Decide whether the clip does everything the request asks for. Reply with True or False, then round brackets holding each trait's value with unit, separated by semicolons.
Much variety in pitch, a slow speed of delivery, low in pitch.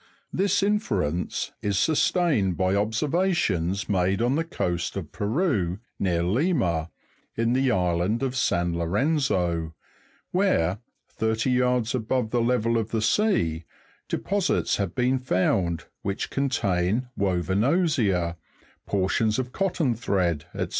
True (6.6 semitones; 120 wpm; 110 Hz)